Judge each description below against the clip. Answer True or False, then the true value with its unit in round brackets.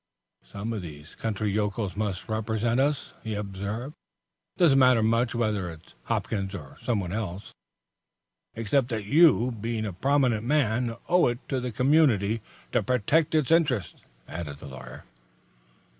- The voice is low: True (110 Hz)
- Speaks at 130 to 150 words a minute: True (145 wpm)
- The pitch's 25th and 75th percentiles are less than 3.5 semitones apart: False (4.1 semitones)